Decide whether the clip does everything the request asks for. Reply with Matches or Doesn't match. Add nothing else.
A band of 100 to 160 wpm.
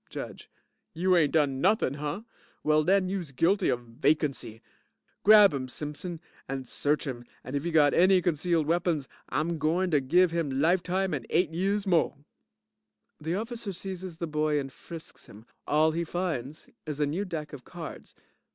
Doesn't match